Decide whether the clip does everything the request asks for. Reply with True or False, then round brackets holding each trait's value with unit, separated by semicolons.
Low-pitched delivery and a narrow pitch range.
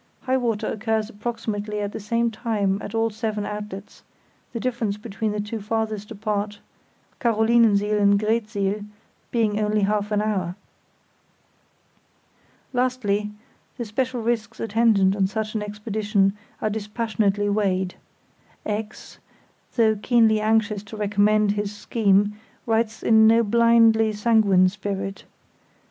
False (215 Hz; 1.6 semitones)